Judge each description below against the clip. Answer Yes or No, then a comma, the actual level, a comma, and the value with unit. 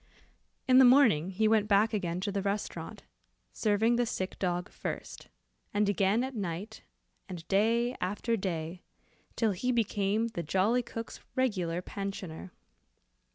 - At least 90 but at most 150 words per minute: Yes, average, 140 wpm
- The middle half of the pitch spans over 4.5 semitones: No, average, 3.6 semitones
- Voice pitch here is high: Yes, high, 205 Hz